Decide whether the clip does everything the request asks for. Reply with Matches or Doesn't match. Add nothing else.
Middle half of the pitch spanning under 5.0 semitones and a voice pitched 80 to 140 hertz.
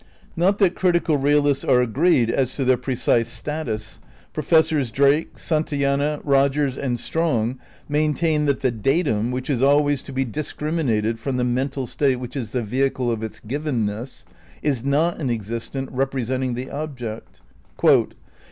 Matches